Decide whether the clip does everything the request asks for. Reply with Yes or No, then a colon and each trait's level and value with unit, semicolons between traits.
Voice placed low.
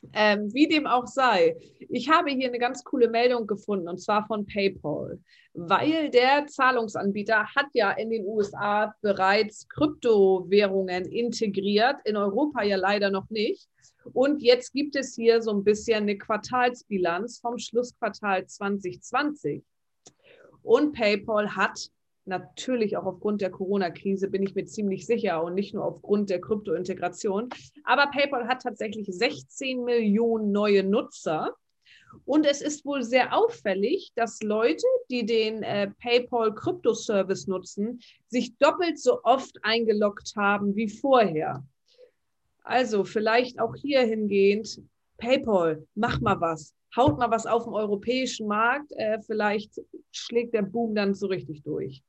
No: high, 220 Hz